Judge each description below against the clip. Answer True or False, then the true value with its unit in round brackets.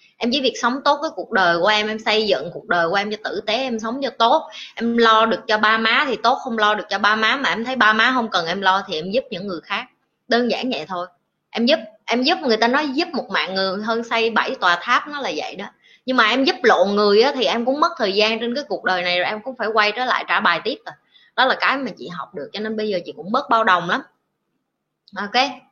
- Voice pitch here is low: False (225 Hz)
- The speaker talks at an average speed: False (290 wpm)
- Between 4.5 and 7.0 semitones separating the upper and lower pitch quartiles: False (3.8 semitones)